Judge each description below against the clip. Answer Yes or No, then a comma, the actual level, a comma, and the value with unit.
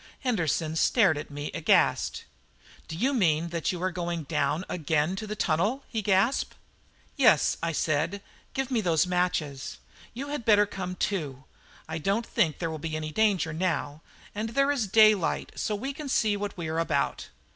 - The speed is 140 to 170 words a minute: No, average, 180 wpm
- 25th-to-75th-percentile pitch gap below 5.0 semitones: No, average, 5.3 semitones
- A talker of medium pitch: Yes, medium, 180 Hz